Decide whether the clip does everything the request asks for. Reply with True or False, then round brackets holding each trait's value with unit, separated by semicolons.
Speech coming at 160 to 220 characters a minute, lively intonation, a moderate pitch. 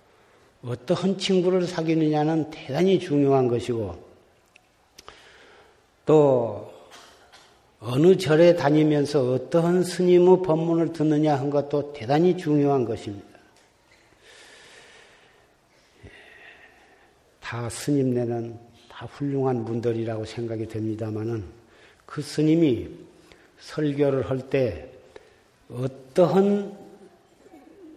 True (185 characters per minute; 6.9 semitones; 145 Hz)